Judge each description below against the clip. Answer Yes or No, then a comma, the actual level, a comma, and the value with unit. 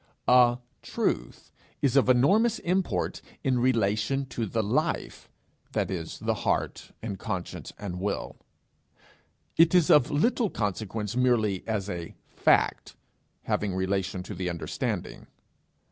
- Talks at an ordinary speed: No, slow, 125 wpm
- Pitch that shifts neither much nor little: No, wide, 5.8 semitones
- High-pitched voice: No, low, 110 Hz